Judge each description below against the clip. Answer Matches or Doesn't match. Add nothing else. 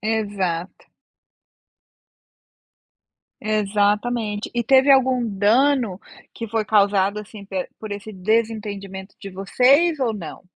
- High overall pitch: Matches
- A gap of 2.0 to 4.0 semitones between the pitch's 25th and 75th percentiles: Matches